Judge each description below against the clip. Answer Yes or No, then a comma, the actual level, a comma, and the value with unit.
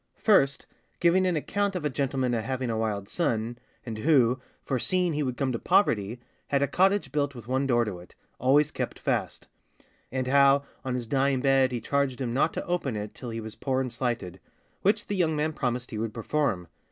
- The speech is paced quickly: Yes, fast, 210 wpm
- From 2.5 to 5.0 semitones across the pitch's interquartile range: Yes, average, 4.0 semitones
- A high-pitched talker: No, low, 130 Hz